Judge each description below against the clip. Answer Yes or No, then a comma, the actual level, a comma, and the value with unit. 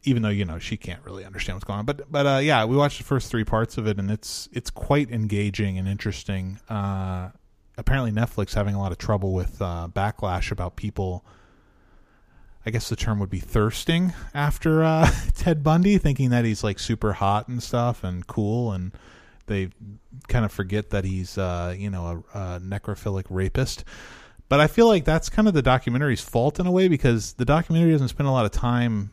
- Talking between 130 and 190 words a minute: No, fast, 205 wpm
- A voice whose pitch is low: Yes, low, 105 Hz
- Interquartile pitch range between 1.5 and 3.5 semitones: No, average, 4.8 semitones